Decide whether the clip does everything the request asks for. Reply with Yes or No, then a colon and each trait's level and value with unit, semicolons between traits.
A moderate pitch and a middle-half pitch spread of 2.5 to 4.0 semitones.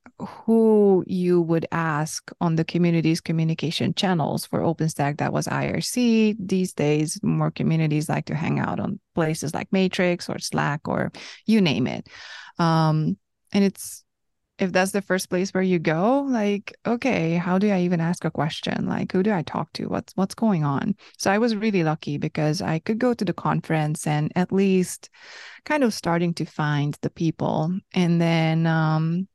Yes: medium, 175 Hz; average, 3.7 semitones